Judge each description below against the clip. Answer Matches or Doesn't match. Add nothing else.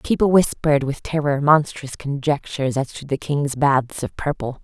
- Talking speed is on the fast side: Doesn't match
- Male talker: Doesn't match